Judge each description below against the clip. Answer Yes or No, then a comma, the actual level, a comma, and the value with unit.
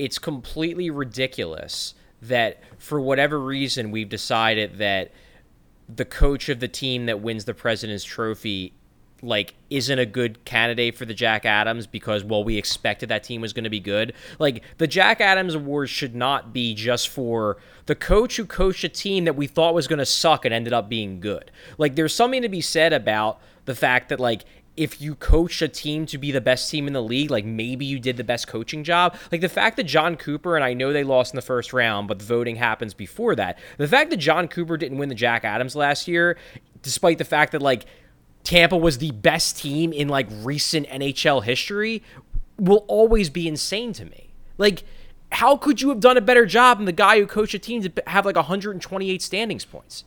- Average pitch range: No, wide, 6.3 semitones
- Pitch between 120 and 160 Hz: Yes, medium, 140 Hz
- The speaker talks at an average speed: No, fast, 210 wpm